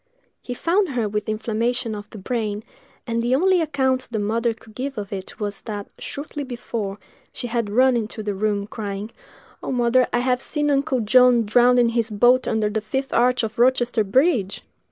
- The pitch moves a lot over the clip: No, average, 3.2 semitones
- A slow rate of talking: No, average, 190 wpm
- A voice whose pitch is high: Yes, high, 235 Hz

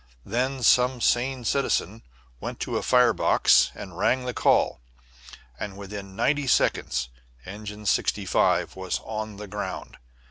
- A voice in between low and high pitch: No, low, 110 Hz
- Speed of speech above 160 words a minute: No, slow, 135 wpm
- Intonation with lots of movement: No, average, 3.9 semitones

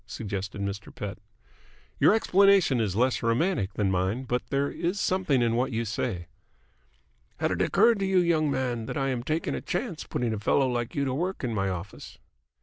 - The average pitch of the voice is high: No, low, 125 Hz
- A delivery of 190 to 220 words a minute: Yes, average, 195 wpm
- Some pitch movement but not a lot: No, wide, 7.4 semitones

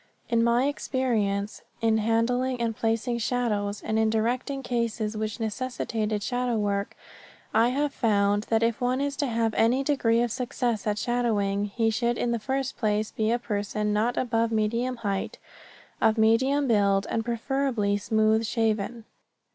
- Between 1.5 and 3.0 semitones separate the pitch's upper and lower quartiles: Yes, narrow, 2.5 semitones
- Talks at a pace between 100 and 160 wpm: Yes, average, 155 wpm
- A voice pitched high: Yes, high, 225 Hz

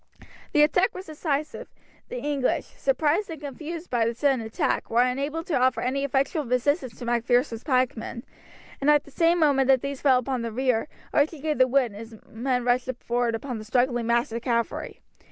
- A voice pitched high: Yes, very high, 260 Hz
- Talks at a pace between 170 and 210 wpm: Yes, average, 190 wpm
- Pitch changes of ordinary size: Yes, average, 3.6 semitones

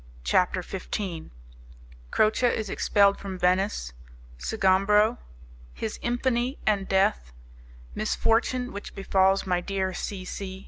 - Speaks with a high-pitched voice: Yes, high, 195 Hz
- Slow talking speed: Yes, slow, 105 wpm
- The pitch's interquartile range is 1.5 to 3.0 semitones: Yes, narrow, 2.6 semitones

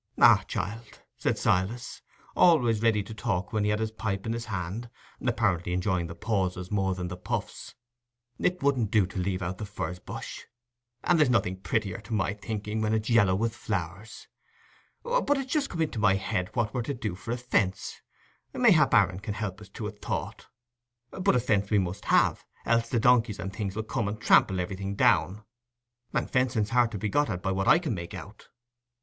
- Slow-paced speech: No, average, 200 wpm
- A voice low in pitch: Yes, low, 105 Hz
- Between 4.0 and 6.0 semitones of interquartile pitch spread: No, average, 3.4 semitones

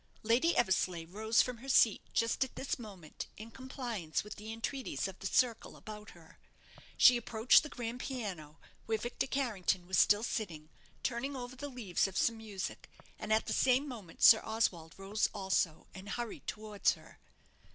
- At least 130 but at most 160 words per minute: No, average, 170 wpm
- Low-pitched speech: No, high, 220 Hz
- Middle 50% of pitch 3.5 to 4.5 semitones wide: Yes, average, 4.2 semitones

